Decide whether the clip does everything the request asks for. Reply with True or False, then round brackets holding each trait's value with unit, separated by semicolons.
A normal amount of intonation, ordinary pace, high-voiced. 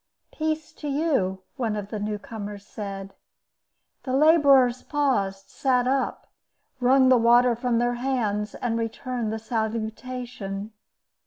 False (3.7 semitones; 130 wpm; 240 Hz)